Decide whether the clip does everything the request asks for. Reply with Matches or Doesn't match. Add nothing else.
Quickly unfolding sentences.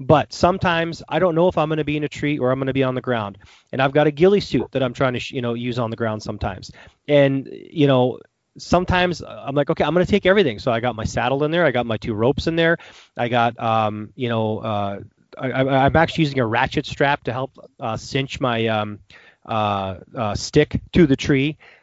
Matches